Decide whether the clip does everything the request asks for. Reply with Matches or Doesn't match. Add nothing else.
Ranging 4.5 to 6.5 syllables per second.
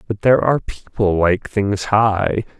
Doesn't match